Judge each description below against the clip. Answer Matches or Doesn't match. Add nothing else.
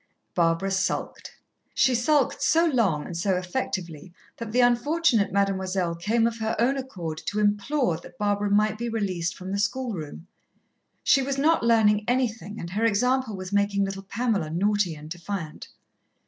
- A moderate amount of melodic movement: Matches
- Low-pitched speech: Doesn't match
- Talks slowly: Doesn't match